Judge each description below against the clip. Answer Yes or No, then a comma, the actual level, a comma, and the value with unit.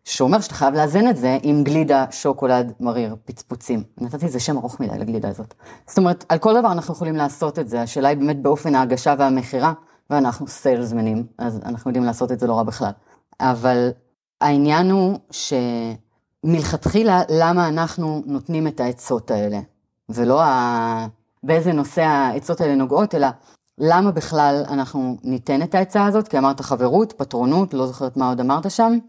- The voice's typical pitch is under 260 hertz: Yes, medium, 140 Hz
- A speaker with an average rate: No, fast, 165 wpm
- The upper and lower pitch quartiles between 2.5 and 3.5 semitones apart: No, average, 4.6 semitones